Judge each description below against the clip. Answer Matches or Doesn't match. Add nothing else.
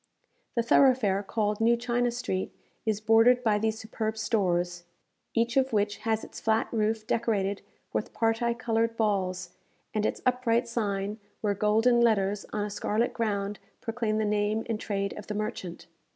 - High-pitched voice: Matches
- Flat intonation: Matches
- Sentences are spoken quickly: Doesn't match